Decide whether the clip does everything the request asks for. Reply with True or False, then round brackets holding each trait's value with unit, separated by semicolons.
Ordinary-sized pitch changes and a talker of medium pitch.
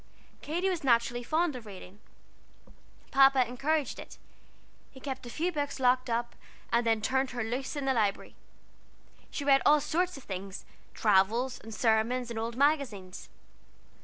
False (3.7 semitones; 250 Hz)